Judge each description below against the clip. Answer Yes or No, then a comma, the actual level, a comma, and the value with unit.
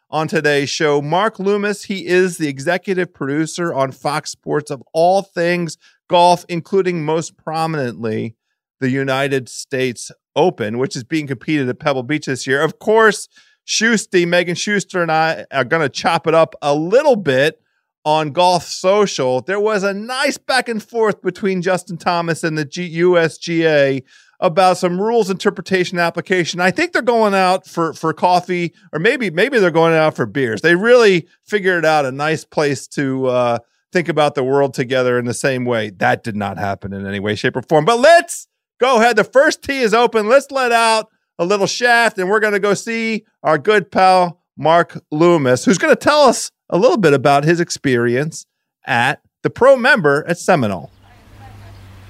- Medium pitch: Yes, medium, 170 Hz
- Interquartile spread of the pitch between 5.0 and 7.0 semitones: Yes, wide, 5.6 semitones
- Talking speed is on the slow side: No, average, 180 wpm